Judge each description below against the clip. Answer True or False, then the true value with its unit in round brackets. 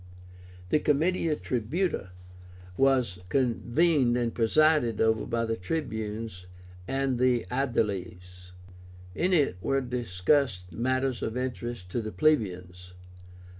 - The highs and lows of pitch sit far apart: False (4.7 semitones)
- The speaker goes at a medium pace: False (100 wpm)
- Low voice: True (120 Hz)